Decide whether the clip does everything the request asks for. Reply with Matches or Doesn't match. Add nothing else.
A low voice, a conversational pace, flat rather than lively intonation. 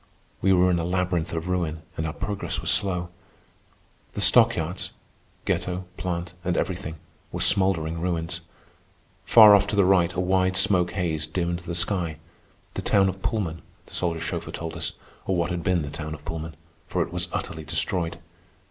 Matches